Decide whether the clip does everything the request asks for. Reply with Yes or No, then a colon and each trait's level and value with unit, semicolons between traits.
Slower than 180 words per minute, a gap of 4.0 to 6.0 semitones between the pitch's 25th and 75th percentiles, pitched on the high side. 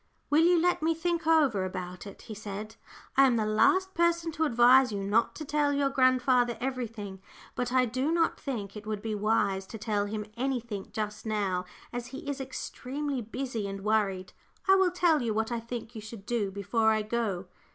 No: average, 200 wpm; average, 4.7 semitones; high, 235 Hz